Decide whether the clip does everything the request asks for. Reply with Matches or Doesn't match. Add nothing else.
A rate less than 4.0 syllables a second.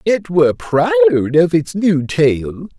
Matches